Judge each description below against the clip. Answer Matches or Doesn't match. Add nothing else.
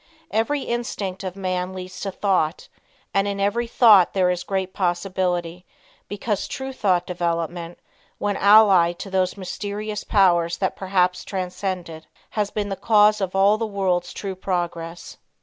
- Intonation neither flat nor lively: Doesn't match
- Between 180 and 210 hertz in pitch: Matches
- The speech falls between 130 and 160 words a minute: Matches